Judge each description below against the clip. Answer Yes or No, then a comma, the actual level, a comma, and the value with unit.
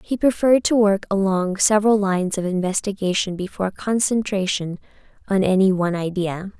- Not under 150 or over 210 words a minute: No, slow, 135 wpm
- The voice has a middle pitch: No, high, 195 Hz